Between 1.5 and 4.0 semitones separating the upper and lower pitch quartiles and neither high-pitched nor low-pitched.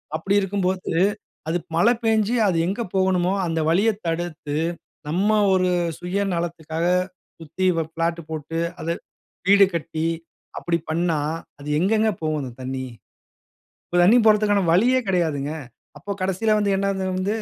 Yes: average, 3.4 semitones; medium, 180 Hz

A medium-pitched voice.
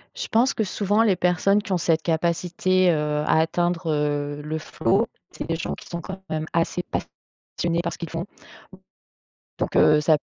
Yes: medium, 170 Hz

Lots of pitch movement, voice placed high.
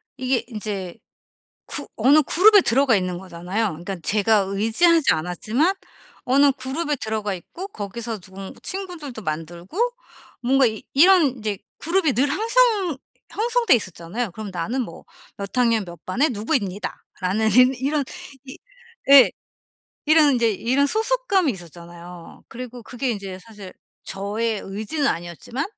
Yes: wide, 6.7 semitones; high, 230 Hz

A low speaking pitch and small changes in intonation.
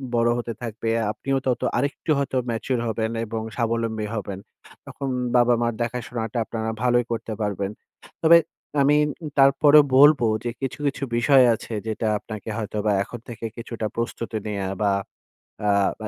Yes: low, 115 Hz; narrow, 2.3 semitones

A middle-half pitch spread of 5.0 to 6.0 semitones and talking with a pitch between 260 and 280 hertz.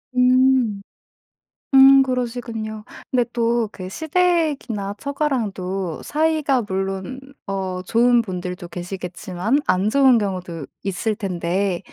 No: wide, 5.5 semitones; high, 215 Hz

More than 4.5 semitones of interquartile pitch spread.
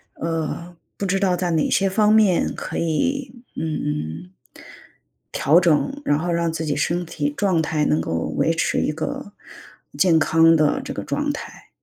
No: average, 3.3 semitones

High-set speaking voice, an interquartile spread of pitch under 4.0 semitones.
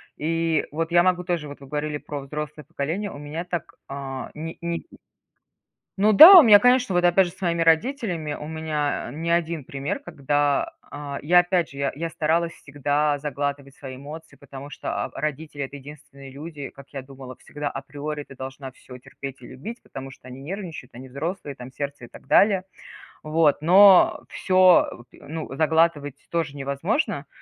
No: medium, 150 Hz; average, 3.4 semitones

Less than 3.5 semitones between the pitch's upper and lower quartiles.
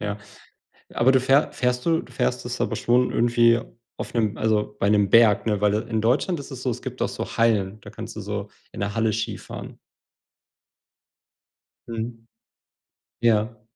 Yes: average, 2.7 semitones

